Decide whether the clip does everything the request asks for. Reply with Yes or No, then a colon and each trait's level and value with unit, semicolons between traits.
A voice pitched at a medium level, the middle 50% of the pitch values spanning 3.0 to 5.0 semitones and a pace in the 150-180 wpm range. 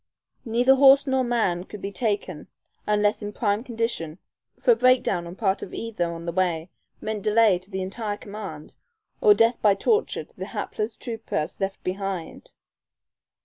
No: high, 210 Hz; average, 3.7 semitones; average, 170 wpm